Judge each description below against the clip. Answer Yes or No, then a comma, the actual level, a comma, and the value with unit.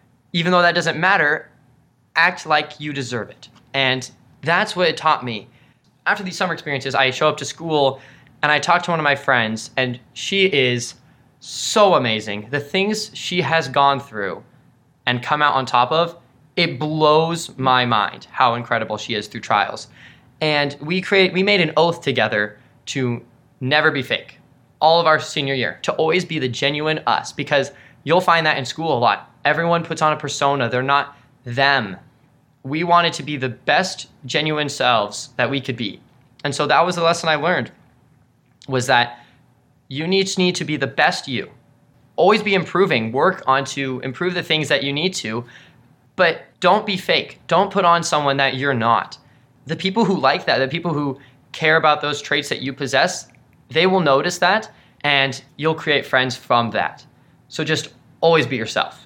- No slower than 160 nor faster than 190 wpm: Yes, average, 185 wpm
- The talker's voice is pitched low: No, medium, 145 Hz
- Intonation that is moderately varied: Yes, average, 4.1 semitones